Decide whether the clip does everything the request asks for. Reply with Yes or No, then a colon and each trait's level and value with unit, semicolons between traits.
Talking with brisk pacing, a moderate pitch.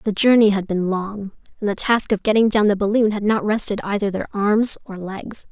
No: fast, 230 wpm; high, 205 Hz